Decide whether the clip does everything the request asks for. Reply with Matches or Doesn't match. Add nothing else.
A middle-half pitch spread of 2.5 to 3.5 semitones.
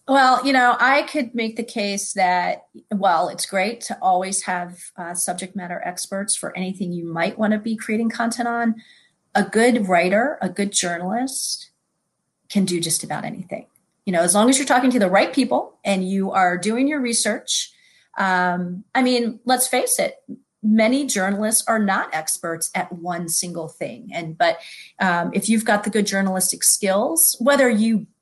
Doesn't match